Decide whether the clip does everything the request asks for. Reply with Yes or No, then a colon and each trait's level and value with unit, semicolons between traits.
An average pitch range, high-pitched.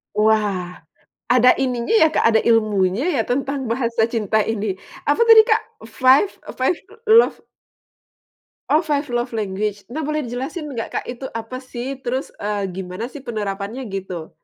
Yes: average, 4.3 semitones; high, 235 Hz